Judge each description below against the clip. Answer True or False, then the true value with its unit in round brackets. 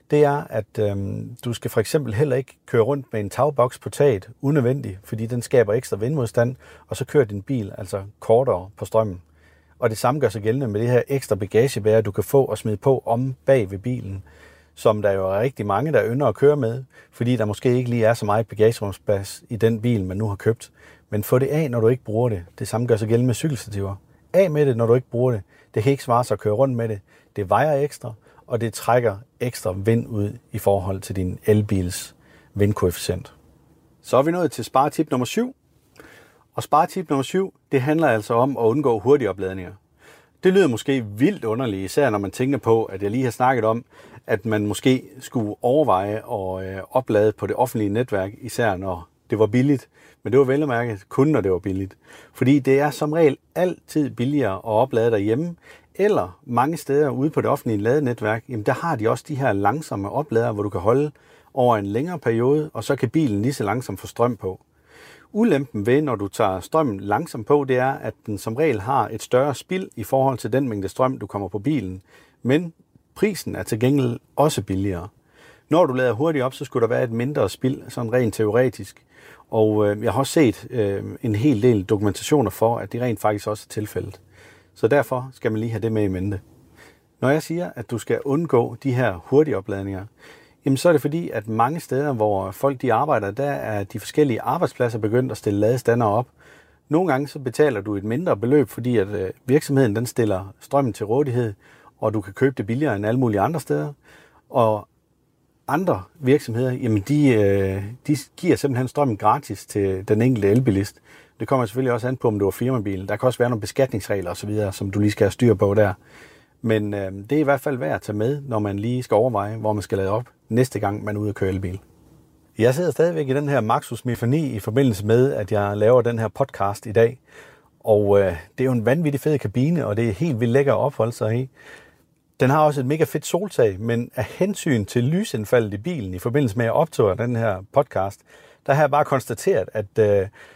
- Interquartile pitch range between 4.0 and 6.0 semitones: True (4.6 semitones)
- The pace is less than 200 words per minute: False (215 wpm)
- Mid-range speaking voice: False (120 Hz)